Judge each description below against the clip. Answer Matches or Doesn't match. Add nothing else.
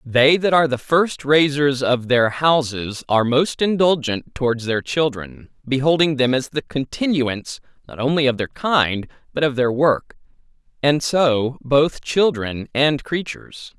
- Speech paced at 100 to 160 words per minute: Matches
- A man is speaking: Matches